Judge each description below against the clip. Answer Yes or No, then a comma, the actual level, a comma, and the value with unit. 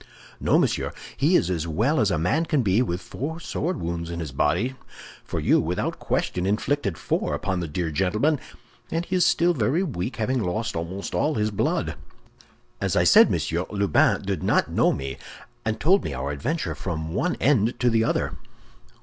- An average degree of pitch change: No, wide, 8.8 semitones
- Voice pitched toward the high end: No, low, 105 Hz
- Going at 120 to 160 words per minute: No, average, 190 wpm